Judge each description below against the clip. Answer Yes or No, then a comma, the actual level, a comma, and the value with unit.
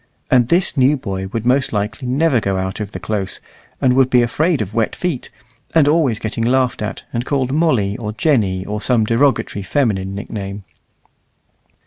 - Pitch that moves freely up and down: No, average, 4.5 semitones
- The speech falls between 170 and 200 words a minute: Yes, average, 175 wpm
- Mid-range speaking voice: No, low, 115 Hz